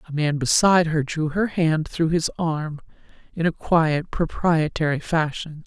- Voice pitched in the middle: Yes, medium, 160 Hz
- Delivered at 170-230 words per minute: No, average, 160 wpm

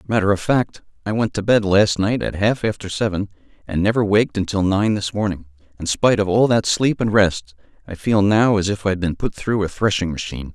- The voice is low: Yes, low, 100 Hz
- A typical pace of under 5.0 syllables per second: No, 5.6 syllables/s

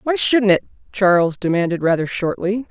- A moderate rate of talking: Yes, average, 155 wpm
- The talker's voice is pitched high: Yes, high, 195 Hz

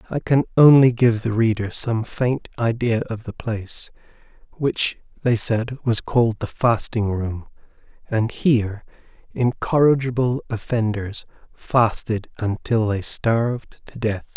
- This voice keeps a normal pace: No, slow, 125 wpm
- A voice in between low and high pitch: No, low, 115 Hz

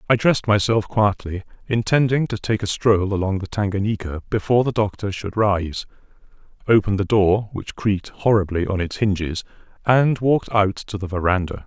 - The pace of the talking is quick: No, average, 165 wpm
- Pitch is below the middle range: Yes, low, 105 Hz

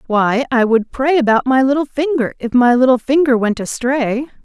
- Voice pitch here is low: No, very high, 255 Hz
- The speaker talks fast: No, average, 190 wpm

